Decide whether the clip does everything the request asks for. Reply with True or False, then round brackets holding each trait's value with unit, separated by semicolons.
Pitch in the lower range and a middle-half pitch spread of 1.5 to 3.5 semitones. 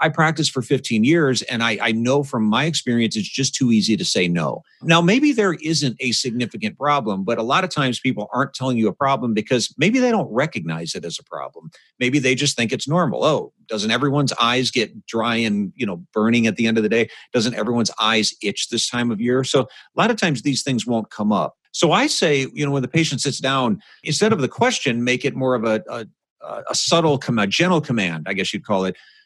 False (130 Hz; 4.5 semitones)